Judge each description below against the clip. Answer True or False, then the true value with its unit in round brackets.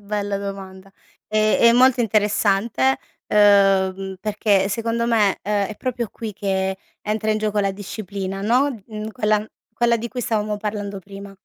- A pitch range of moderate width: False (2.0 semitones)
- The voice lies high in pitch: True (210 Hz)